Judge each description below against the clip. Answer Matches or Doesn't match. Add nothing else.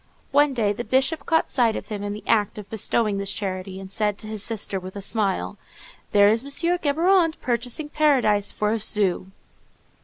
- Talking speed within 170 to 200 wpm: Matches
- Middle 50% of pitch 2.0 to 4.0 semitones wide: Doesn't match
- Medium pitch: Doesn't match